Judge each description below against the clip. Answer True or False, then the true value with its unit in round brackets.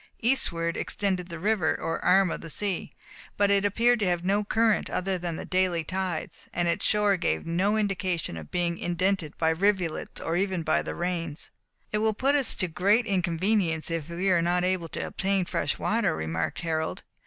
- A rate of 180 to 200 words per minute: True (190 wpm)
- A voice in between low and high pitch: True (180 Hz)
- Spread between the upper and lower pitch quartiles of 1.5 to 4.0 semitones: True (3.2 semitones)